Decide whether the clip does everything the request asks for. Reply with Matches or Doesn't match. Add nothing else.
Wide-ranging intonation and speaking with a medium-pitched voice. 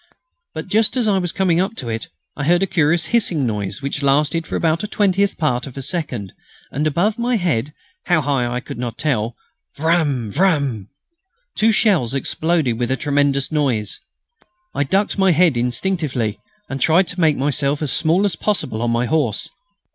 Matches